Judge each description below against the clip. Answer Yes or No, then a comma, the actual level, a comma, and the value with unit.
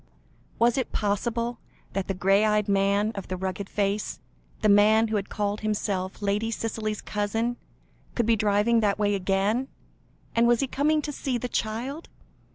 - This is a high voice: Yes, high, 215 Hz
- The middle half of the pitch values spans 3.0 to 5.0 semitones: No, narrow, 2.5 semitones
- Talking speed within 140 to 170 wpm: Yes, average, 165 wpm